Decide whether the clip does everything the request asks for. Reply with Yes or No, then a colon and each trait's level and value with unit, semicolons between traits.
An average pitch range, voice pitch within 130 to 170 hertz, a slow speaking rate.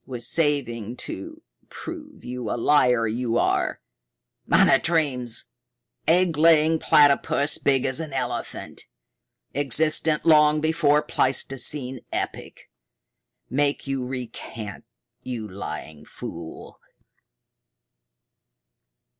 Yes: average, 4.0 semitones; low, 135 Hz; slow, 90 wpm